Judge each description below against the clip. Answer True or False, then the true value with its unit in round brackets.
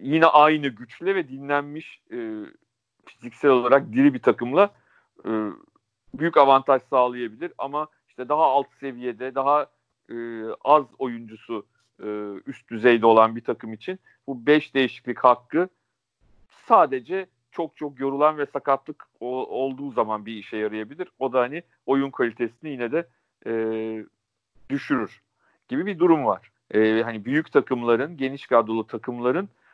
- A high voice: False (135 Hz)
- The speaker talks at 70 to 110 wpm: False (135 wpm)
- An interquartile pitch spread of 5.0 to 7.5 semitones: False (4.6 semitones)